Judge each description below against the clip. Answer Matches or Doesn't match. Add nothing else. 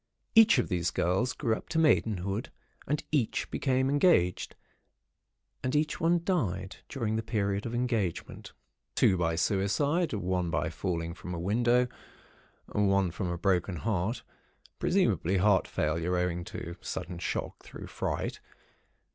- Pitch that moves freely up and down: Matches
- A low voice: Matches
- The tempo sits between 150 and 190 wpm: Doesn't match